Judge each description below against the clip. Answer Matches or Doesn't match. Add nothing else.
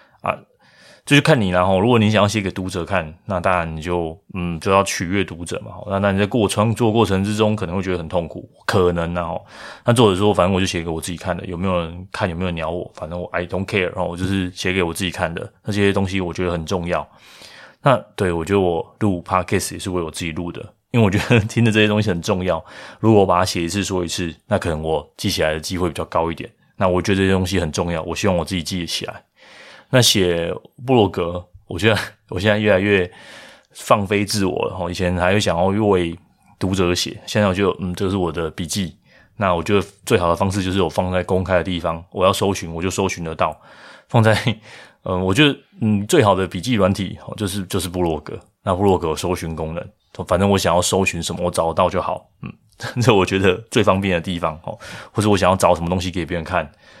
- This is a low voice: Matches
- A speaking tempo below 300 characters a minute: Doesn't match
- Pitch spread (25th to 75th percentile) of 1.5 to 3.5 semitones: Matches